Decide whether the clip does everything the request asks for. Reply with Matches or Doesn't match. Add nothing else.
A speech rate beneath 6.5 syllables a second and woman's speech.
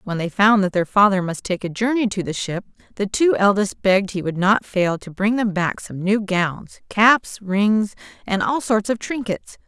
Matches